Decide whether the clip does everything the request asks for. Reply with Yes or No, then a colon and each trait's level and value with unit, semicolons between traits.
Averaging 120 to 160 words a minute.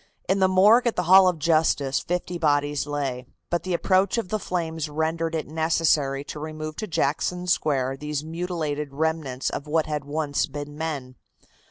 No: average, 175 wpm